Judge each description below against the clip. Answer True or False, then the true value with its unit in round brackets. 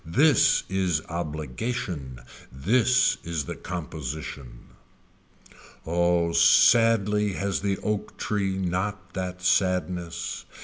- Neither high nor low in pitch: False (90 Hz)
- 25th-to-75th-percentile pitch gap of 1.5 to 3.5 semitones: True (3.2 semitones)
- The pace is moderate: False (90 wpm)